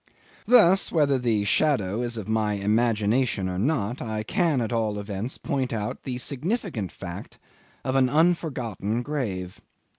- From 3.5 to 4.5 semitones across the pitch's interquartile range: No, average, 5.1 semitones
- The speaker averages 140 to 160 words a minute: Yes, average, 145 wpm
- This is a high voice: No, low, 120 Hz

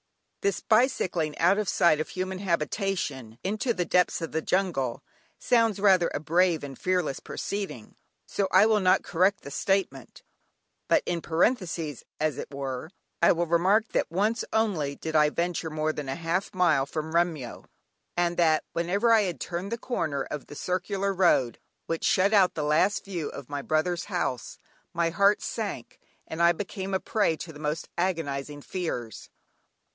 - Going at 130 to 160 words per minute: No, average, 170 wpm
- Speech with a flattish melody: No, average, 4.1 semitones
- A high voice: No, medium, 170 Hz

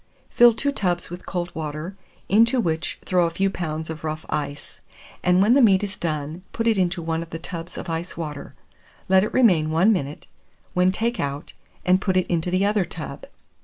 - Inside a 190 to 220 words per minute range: Yes, average, 200 wpm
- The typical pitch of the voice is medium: Yes, medium, 175 Hz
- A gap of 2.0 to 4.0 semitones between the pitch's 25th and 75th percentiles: Yes, average, 3.4 semitones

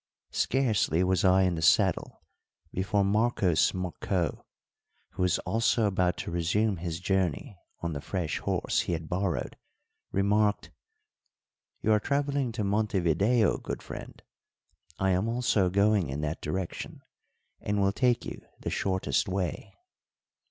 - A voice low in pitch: Yes, very low, 95 Hz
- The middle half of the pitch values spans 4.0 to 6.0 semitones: No, average, 3.2 semitones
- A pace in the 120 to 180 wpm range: Yes, slow, 135 wpm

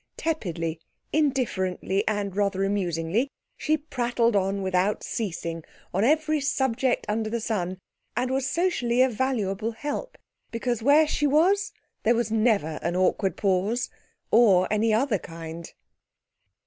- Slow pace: Yes, slow, 130 wpm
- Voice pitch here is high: Yes, high, 220 Hz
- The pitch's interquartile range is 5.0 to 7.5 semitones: Yes, wide, 5.6 semitones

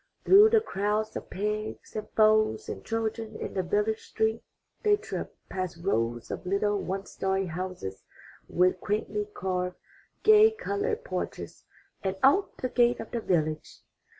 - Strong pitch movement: No, average, 3.6 semitones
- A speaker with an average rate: Yes, average, 150 wpm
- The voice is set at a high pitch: Yes, high, 210 Hz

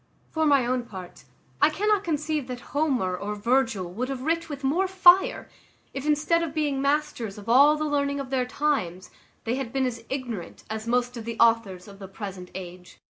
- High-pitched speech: Yes, very high, 255 Hz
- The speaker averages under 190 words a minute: No, average, 195 wpm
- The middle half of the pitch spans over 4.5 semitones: Yes, wide, 5.5 semitones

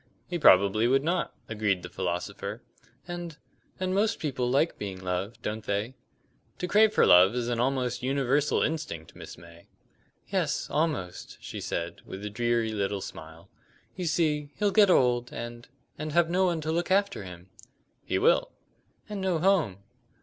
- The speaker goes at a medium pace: Yes, average, 165 wpm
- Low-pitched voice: Yes, low, 125 Hz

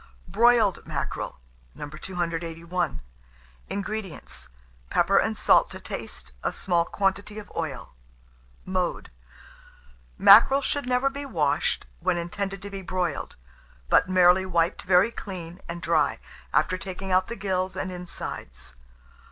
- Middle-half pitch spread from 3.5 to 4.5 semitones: No, average, 3.0 semitones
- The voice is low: No, medium, 185 Hz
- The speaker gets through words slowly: Yes, slow, 120 wpm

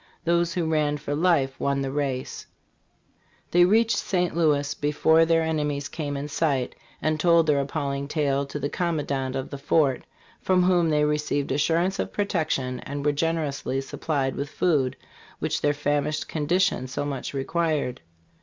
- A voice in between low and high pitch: Yes, medium, 150 Hz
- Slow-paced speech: No, average, 165 wpm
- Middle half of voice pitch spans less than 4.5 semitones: Yes, average, 2.8 semitones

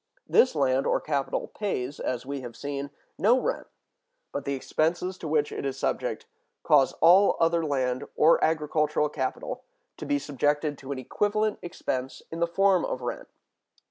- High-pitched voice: No, medium, 150 Hz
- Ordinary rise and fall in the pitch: Yes, average, 3.8 semitones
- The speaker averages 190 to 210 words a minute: No, average, 165 wpm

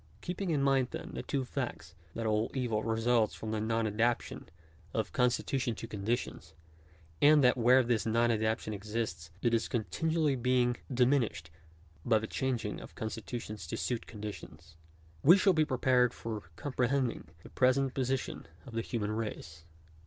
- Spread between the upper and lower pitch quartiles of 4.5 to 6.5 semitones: No, average, 3.0 semitones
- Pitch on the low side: Yes, low, 115 Hz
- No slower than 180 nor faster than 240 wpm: No, average, 165 wpm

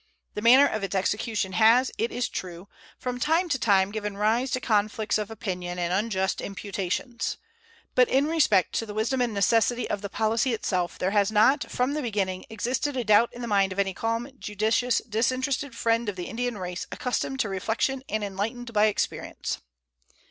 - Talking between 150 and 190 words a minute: Yes, average, 185 wpm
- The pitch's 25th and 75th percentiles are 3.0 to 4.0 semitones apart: Yes, average, 3.6 semitones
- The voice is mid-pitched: No, high, 220 Hz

